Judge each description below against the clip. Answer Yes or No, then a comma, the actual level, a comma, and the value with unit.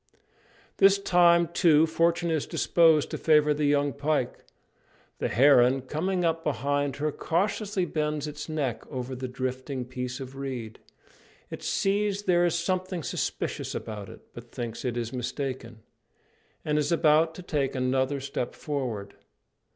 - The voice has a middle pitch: Yes, medium, 145 Hz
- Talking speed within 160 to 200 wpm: No, average, 145 wpm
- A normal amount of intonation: Yes, average, 4.4 semitones